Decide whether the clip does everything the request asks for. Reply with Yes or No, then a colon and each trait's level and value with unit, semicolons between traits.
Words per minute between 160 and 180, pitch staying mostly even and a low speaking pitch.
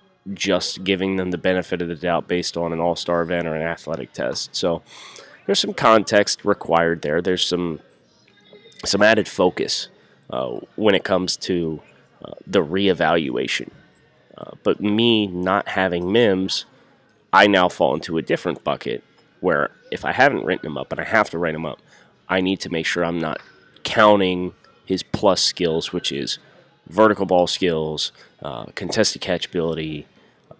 Yes: average, 165 wpm; narrow, 2.3 semitones; very low, 90 Hz